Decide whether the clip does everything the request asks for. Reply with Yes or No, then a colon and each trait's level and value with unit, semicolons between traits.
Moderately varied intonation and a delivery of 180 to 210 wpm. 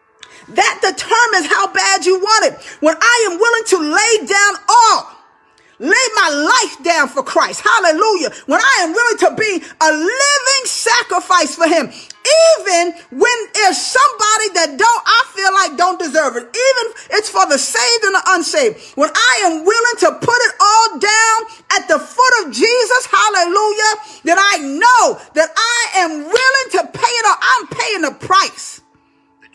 No: average, 4.8 semitones; average, 170 wpm